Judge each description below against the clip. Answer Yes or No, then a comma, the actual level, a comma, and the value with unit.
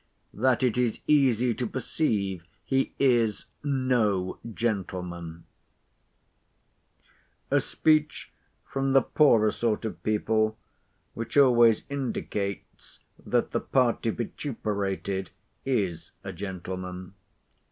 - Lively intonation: No, average, 4.9 semitones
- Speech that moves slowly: Yes, slow, 95 wpm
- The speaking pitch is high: No, low, 110 Hz